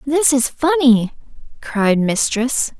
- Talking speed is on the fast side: No, slow, 105 wpm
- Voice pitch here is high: Yes, very high, 260 Hz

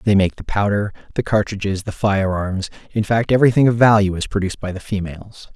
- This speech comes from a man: Yes, male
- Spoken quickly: No, average, 195 wpm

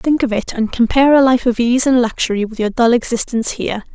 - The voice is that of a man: No, female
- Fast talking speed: Yes, fast, 245 wpm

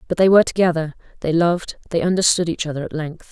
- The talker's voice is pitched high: No, medium, 165 Hz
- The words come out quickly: Yes, fast, 215 wpm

